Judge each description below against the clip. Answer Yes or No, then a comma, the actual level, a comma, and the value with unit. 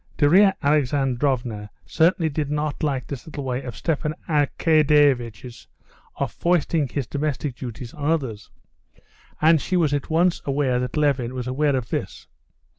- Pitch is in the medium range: Yes, medium, 145 Hz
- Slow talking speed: No, average, 145 wpm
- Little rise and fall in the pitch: No, average, 3.3 semitones